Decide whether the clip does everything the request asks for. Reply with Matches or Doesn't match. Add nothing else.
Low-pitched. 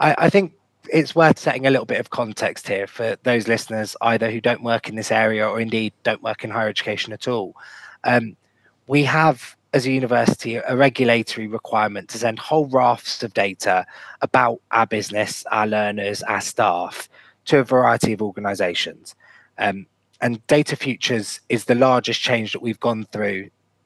Matches